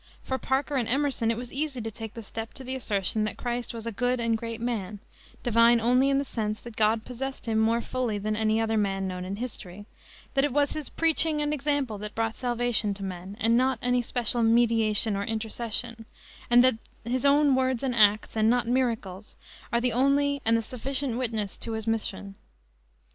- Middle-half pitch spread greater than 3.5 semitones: No, average, 2.8 semitones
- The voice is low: No, high, 230 Hz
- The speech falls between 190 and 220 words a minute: Yes, fast, 205 wpm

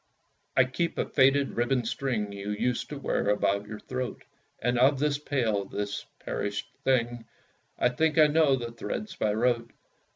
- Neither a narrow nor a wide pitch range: Yes, average, 4.4 semitones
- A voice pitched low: Yes, low, 125 Hz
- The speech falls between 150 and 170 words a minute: Yes, average, 165 wpm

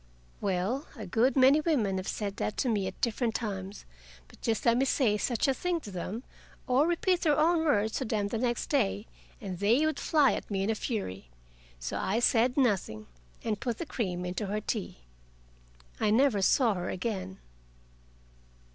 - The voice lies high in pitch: Yes, high, 220 Hz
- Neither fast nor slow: Yes, average, 185 wpm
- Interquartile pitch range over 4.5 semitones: Yes, average, 5.1 semitones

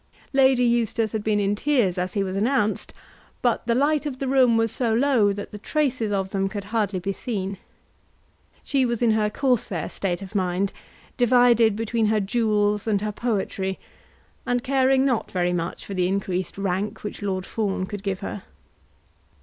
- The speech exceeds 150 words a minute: Yes, average, 180 wpm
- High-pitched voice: Yes, high, 210 Hz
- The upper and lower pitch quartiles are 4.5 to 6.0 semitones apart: No, average, 3.7 semitones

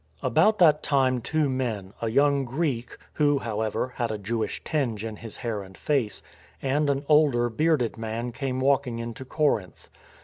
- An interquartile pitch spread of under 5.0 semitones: Yes, average, 4.0 semitones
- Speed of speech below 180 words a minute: Yes, average, 170 wpm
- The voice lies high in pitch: No, low, 125 Hz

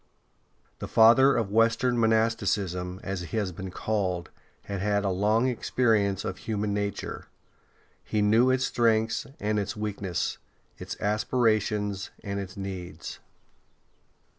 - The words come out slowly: Yes, slow, 125 wpm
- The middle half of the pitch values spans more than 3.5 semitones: No, narrow, 2.5 semitones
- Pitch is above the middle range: No, low, 105 Hz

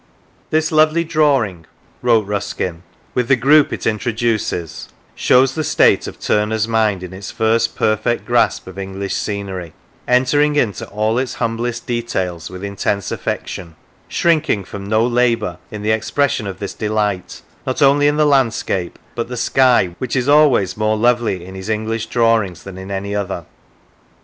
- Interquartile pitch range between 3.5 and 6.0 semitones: Yes, average, 4.2 semitones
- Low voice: Yes, low, 110 Hz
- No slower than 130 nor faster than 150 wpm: No, average, 165 wpm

